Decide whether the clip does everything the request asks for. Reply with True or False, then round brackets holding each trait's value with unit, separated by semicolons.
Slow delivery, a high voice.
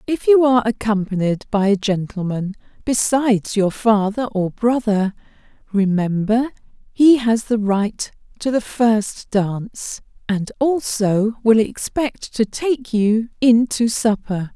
True (130 wpm; 220 Hz)